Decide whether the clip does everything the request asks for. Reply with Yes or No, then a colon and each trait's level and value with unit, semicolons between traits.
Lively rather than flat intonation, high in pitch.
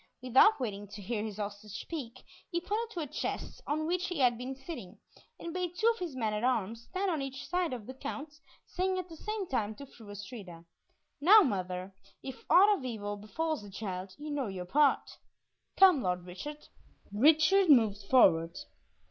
Yes: wide, 8.0 semitones; very high, 260 Hz